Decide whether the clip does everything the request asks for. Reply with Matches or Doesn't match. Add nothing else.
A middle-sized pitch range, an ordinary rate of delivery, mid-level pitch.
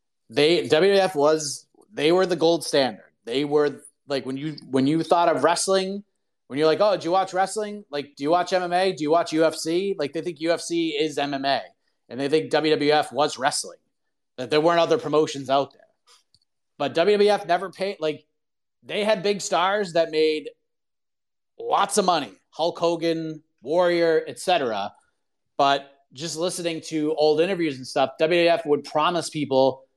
Matches